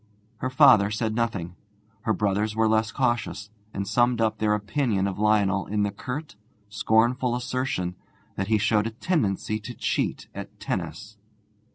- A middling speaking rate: Yes, average, 155 wpm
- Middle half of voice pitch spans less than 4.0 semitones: Yes, average, 2.9 semitones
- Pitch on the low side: Yes, low, 110 Hz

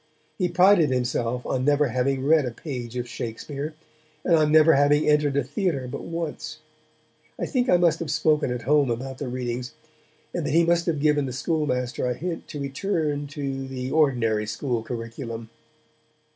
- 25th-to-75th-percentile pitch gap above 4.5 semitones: No, average, 3.8 semitones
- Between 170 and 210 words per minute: Yes, average, 175 wpm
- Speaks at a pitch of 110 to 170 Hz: Yes, medium, 140 Hz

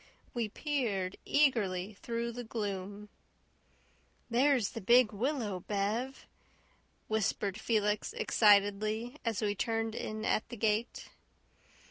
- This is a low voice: No, high, 220 Hz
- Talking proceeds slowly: Yes, slow, 105 wpm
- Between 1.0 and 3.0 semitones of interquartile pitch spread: Yes, average, 2.7 semitones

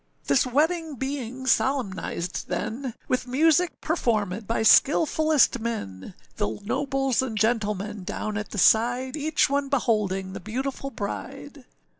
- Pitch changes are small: No, average, 4.8 semitones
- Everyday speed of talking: No, slow, 125 wpm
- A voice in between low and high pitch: No, high, 240 Hz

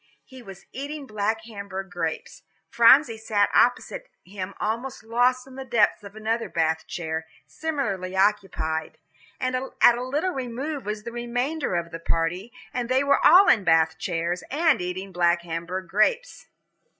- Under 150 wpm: No, average, 155 wpm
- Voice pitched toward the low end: No, high, 215 Hz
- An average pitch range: No, wide, 6.2 semitones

